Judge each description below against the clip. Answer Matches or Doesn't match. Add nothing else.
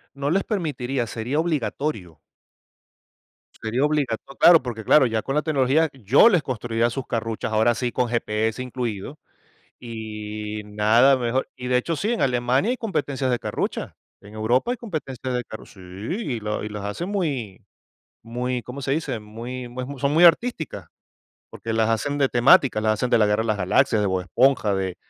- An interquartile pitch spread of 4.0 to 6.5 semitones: Matches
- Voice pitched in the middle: Doesn't match